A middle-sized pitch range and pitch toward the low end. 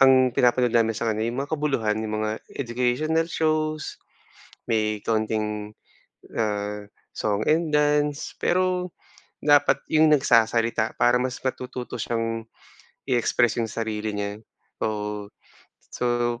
Yes: average, 4.9 semitones; low, 120 Hz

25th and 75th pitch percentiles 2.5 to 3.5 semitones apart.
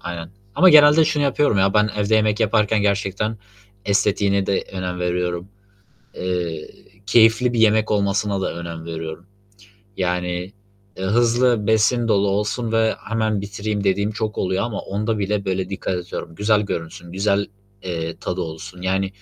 Yes: average, 3.1 semitones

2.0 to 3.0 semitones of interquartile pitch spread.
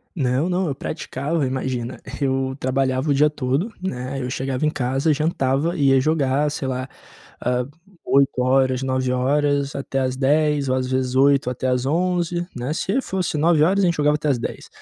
Yes: average, 2.7 semitones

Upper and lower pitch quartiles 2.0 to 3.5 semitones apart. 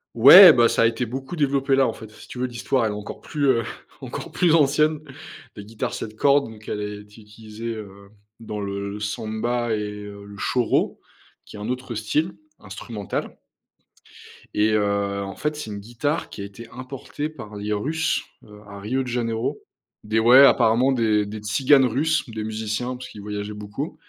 No: average, 4.1 semitones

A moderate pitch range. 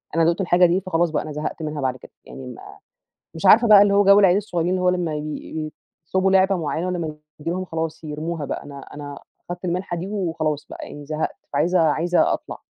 Yes: average, 3.2 semitones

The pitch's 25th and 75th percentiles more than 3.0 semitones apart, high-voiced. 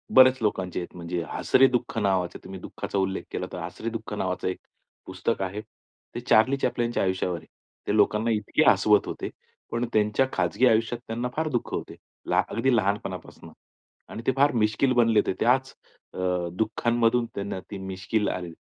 No: average, 3.8 semitones; low, 110 Hz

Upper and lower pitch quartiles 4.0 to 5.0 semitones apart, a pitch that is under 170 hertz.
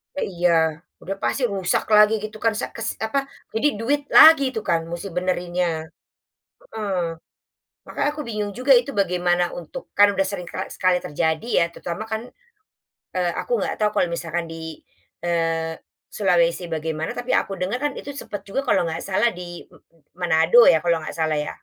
No: average, 4.3 semitones; medium, 185 Hz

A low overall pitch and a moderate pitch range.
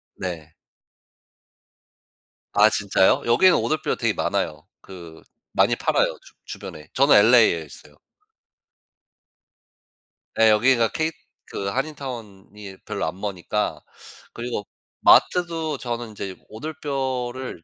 No: low, 110 Hz; wide, 5.7 semitones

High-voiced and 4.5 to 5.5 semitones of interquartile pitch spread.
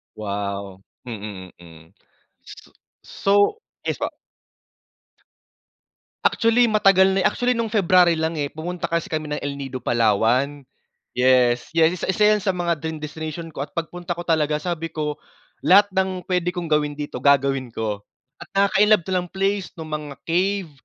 No: medium, 160 Hz; average, 5.0 semitones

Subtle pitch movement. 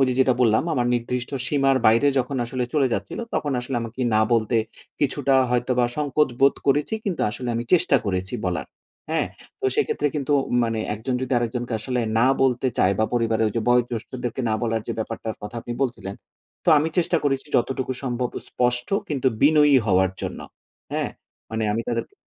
No: average, 3.0 semitones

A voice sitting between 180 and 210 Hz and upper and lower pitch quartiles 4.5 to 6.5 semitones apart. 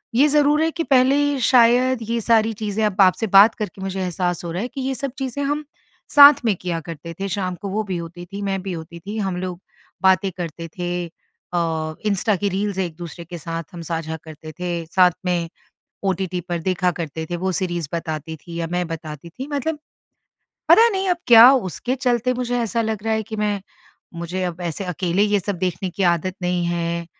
Yes: medium, 185 Hz; average, 4.8 semitones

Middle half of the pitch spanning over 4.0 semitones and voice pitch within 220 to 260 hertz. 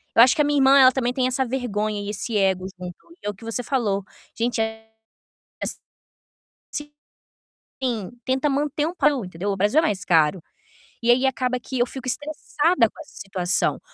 Yes: average, 4.7 semitones; high, 240 Hz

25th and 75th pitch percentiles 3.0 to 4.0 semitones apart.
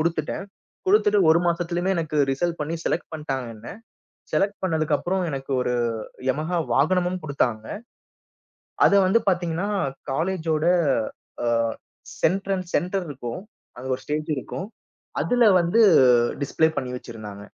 No: average, 4.7 semitones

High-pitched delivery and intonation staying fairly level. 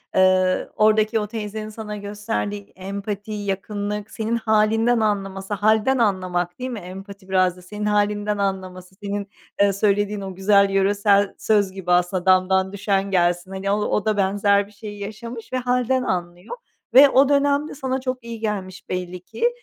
Yes: high, 205 Hz; narrow, 2.3 semitones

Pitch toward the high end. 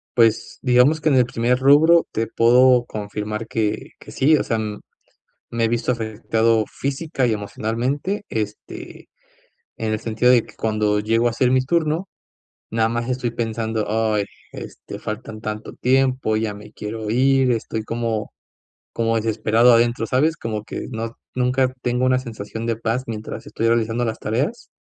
No: low, 115 Hz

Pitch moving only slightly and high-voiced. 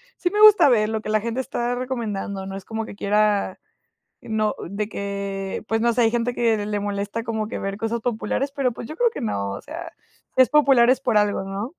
No: average, 3.4 semitones; high, 225 Hz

